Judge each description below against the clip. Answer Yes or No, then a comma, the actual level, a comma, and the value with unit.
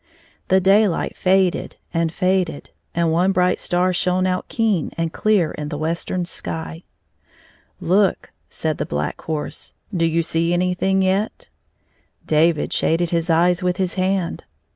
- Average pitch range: No, narrow, 2.3 semitones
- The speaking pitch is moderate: Yes, medium, 175 Hz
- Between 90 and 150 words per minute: Yes, average, 145 wpm